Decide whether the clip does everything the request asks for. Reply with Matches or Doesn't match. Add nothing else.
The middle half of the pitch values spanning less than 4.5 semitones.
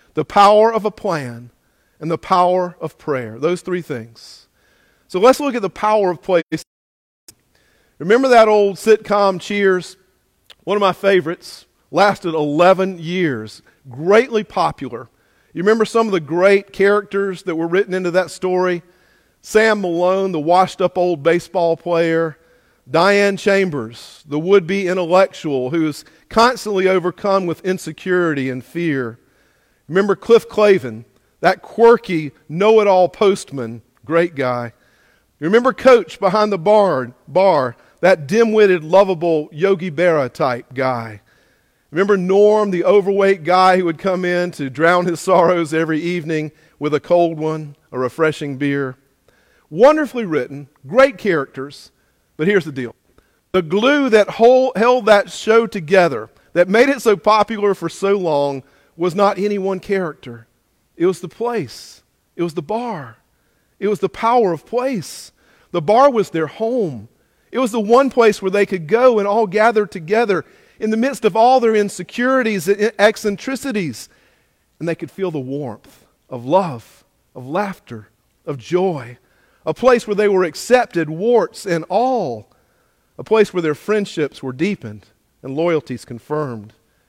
Doesn't match